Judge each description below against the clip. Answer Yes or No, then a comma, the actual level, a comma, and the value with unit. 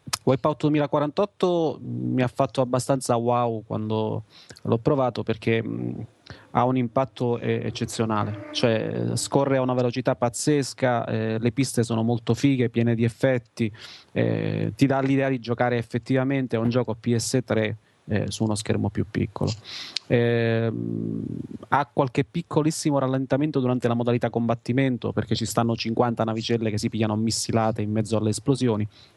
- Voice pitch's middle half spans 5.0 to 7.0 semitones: No, average, 2.9 semitones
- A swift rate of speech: No, average, 140 wpm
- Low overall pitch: Yes, low, 120 Hz